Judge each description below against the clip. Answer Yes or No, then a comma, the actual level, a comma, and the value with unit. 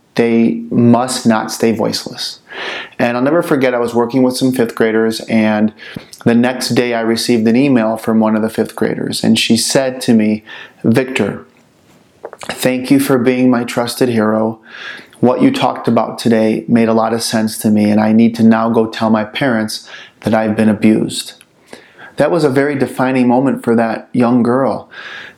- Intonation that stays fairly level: Yes, narrow, 2.1 semitones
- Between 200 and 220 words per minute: No, average, 185 wpm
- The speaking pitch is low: Yes, low, 115 Hz